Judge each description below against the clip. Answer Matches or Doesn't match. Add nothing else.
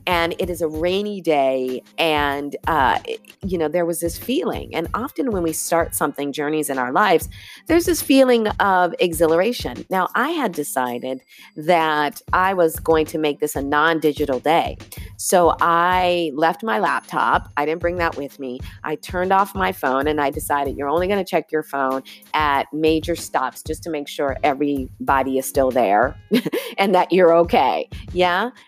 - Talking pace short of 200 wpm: Matches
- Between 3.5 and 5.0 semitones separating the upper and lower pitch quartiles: Matches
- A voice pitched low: Doesn't match